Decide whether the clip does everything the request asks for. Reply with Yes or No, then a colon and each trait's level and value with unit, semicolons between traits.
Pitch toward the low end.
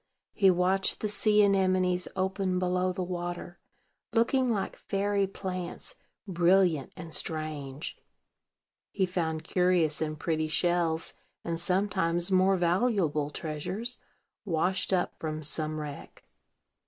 No: medium, 180 Hz